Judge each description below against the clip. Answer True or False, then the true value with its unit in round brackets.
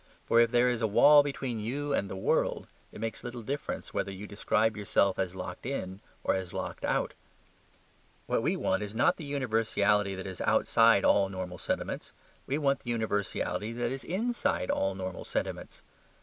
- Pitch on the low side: True (110 Hz)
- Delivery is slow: False (180 wpm)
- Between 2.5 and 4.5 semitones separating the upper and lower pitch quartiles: False (5.0 semitones)